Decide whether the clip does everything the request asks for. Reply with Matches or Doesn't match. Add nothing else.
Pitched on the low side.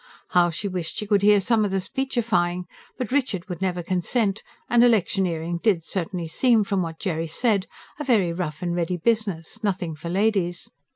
Doesn't match